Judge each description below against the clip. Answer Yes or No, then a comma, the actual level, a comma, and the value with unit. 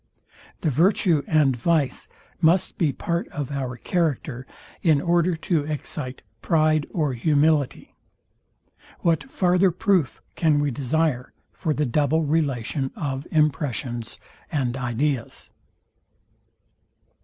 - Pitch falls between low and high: Yes, medium, 150 Hz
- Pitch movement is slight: No, average, 3.6 semitones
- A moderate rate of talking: No, slow, 110 wpm